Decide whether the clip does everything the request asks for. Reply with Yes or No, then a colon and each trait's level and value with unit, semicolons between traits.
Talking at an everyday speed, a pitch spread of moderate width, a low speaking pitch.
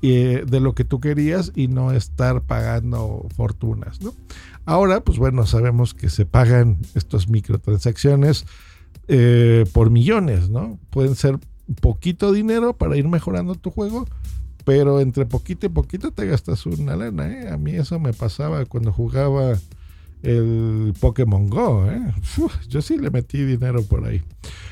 Yes: average, 150 wpm; average, 4.5 semitones; low, 120 Hz